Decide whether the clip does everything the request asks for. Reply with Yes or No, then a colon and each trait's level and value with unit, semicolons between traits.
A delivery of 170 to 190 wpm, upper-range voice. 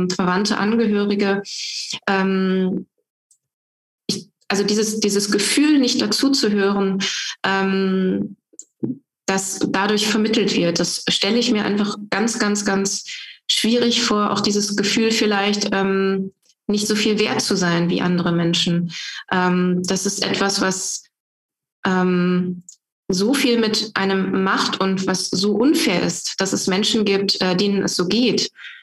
No: average, 135 wpm; high, 200 Hz